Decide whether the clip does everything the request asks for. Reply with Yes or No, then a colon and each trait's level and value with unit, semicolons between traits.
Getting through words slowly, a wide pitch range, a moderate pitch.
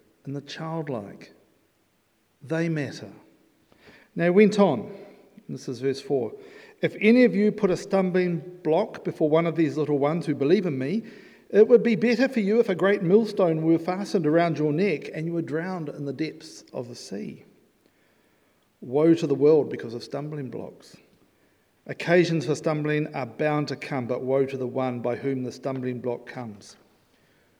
No: average, 180 wpm; wide, 6.0 semitones; medium, 160 Hz